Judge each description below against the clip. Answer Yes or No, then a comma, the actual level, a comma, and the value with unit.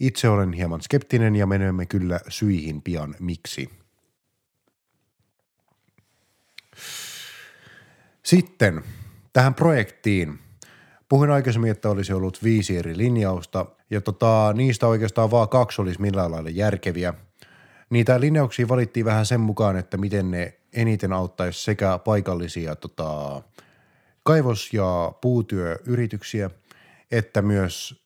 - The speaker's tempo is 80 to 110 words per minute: Yes, average, 105 wpm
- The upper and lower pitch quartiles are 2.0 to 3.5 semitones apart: No, average, 4.3 semitones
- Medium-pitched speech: No, low, 105 Hz